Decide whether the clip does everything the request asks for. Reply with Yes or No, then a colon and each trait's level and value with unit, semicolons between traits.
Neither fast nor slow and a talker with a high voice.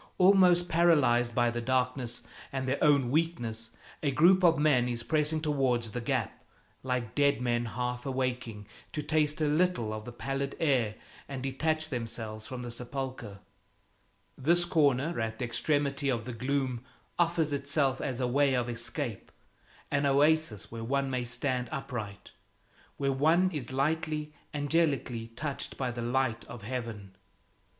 No: average, 150 wpm; low, 130 Hz